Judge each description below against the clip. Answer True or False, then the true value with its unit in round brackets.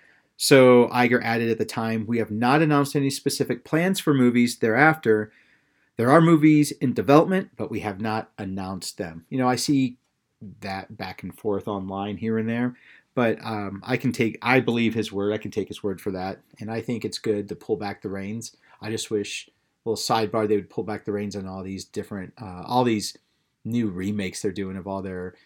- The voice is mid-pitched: False (110 Hz)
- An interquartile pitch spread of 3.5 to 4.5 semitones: True (3.8 semitones)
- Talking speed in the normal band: False (215 wpm)